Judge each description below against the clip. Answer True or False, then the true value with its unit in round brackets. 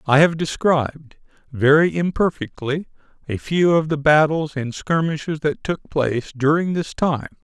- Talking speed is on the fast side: False (145 wpm)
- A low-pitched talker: False (150 Hz)